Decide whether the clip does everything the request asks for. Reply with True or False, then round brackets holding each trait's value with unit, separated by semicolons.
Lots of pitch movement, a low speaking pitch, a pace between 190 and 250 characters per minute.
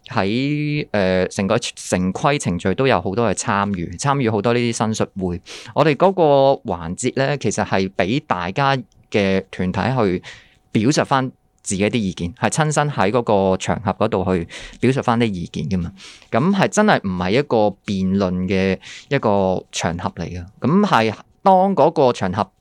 True (5.7 semitones; 105 Hz; 245 characters per minute)